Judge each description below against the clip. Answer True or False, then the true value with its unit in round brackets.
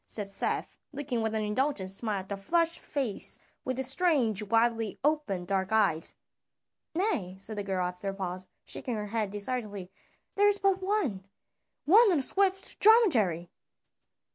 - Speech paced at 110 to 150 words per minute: False (160 wpm)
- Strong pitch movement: True (7.5 semitones)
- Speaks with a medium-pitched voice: False (220 Hz)